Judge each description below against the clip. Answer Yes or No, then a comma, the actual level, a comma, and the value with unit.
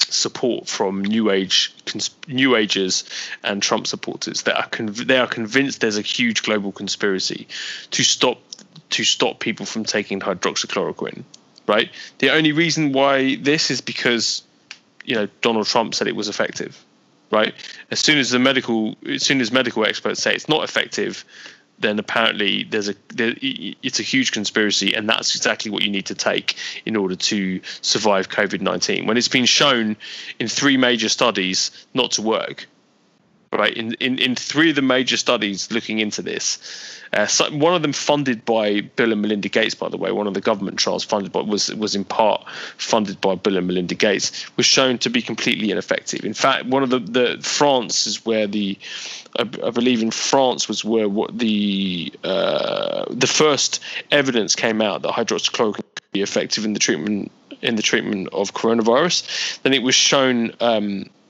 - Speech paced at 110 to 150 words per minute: No, average, 180 wpm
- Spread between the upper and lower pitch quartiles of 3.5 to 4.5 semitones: Yes, average, 4.2 semitones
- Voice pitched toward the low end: Yes, low, 115 Hz